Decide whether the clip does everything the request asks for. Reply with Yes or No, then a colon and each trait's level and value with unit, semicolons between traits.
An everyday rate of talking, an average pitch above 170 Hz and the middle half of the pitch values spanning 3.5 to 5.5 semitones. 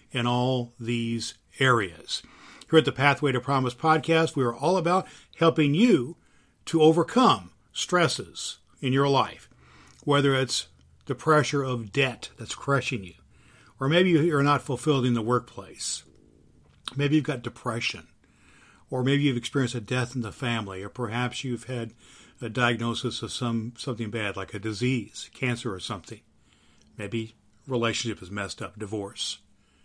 No: average, 150 wpm; low, 120 Hz; average, 4.1 semitones